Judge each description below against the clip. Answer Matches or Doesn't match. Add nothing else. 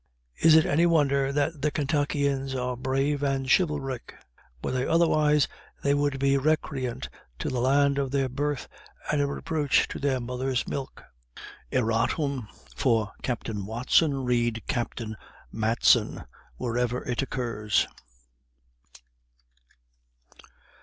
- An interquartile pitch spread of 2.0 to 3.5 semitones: Matches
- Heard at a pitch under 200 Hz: Matches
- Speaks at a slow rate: Matches